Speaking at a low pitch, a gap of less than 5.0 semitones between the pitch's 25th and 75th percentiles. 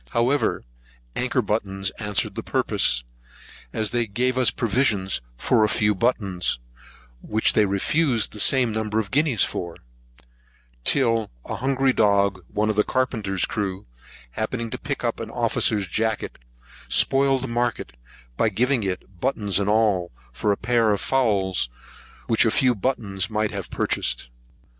Yes: low, 110 Hz; average, 3.7 semitones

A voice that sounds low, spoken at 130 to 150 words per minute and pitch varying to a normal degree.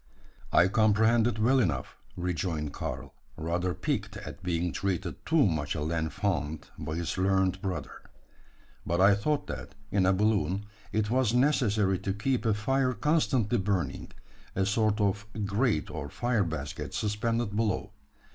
Yes: low, 100 Hz; average, 145 wpm; average, 4.3 semitones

